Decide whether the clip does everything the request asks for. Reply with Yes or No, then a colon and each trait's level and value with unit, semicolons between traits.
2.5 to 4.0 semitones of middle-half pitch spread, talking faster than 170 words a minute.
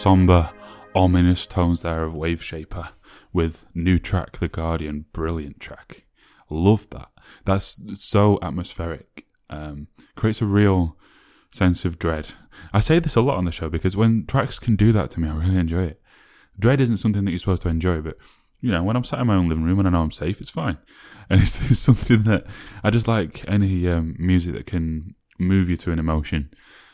Yes: average, 3.7 semitones; average, 200 wpm